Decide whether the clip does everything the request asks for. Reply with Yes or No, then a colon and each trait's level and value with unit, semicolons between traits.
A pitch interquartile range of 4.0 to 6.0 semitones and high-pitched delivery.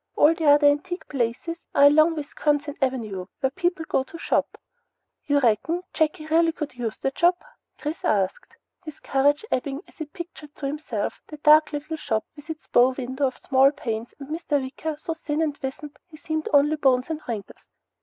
No: average, 2.9 semitones; very high, 290 Hz